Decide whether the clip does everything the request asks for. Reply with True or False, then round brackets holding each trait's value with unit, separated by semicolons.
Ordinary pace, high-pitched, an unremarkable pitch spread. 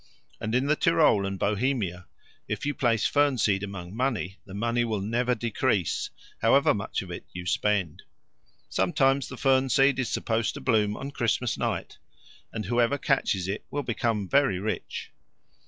False (165 wpm; 115 Hz; 4.9 semitones)